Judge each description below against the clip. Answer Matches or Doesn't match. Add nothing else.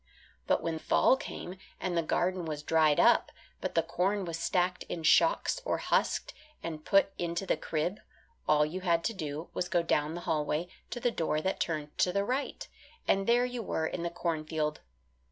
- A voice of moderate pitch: Matches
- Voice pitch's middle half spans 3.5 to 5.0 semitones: Doesn't match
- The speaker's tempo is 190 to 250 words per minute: Matches